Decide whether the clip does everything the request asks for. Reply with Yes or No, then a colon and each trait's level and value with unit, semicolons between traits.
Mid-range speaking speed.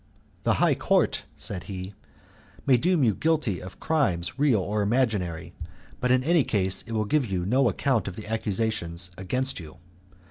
Yes: average, 170 wpm